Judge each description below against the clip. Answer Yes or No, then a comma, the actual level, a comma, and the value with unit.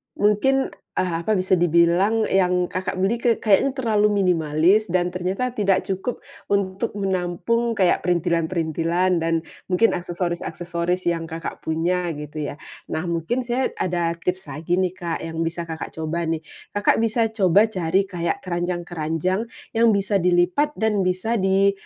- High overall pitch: No, medium, 180 Hz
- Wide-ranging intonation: No, average, 3.0 semitones